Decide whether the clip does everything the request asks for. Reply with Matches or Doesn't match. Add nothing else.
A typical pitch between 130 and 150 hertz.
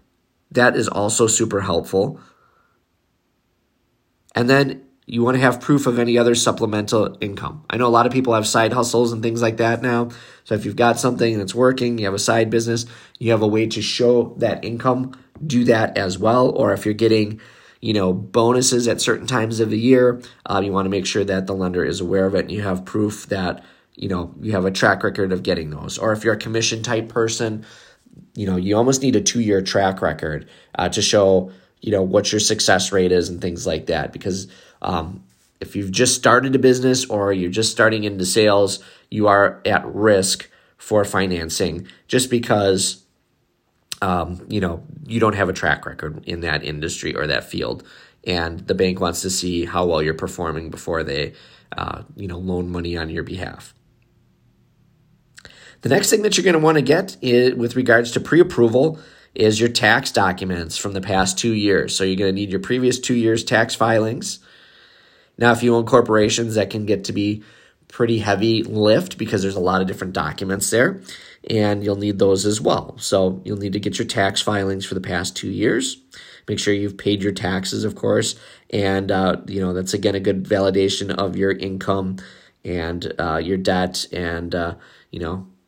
Doesn't match